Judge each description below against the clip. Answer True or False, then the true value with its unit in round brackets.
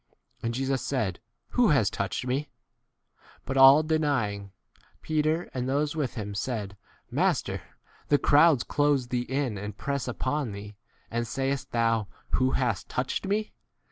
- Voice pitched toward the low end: True (130 Hz)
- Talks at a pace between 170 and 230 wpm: False (150 wpm)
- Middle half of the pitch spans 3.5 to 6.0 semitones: True (4.1 semitones)